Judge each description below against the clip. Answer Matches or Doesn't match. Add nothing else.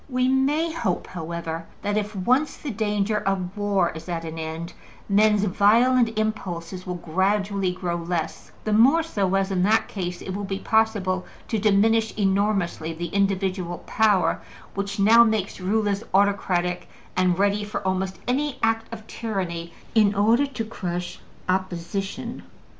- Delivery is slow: Doesn't match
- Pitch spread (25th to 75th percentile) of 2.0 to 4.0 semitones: Matches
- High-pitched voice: Matches